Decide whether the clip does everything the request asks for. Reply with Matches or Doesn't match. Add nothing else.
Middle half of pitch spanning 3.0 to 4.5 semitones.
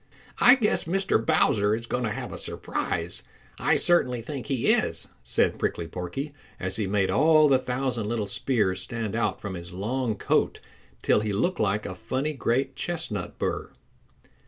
Doesn't match